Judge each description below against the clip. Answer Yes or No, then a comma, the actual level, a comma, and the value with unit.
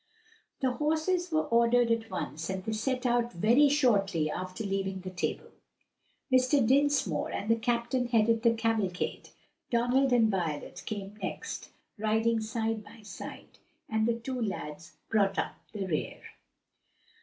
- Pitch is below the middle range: No, high, 225 Hz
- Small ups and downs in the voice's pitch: No, average, 3.8 semitones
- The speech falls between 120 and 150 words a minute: Yes, average, 145 wpm